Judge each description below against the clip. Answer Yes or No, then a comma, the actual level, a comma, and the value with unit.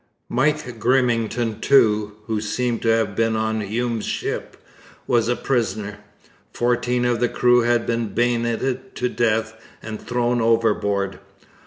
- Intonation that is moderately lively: No, narrow, 1.8 semitones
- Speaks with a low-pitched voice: Yes, low, 115 Hz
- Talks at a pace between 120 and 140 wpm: Yes, slow, 135 wpm